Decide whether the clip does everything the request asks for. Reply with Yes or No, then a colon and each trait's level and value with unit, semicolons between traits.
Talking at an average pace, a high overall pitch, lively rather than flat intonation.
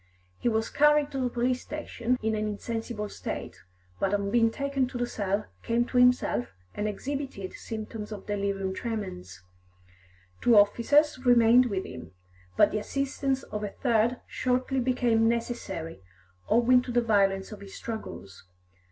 No: average, 150 wpm; high, 230 Hz; average, 3.5 semitones